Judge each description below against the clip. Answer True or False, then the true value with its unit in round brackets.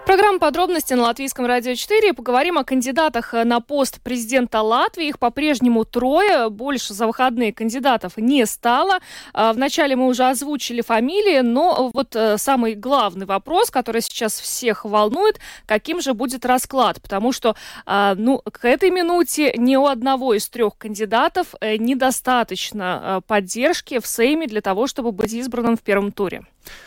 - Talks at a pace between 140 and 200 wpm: True (145 wpm)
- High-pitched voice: True (250 Hz)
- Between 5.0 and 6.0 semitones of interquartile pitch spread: False (3.9 semitones)